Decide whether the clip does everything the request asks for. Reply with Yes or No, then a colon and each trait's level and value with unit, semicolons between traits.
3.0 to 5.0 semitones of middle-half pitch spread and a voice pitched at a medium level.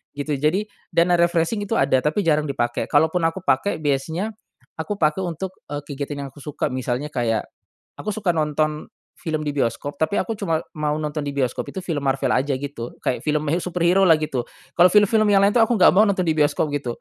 Yes: average, 4.0 semitones; medium, 155 Hz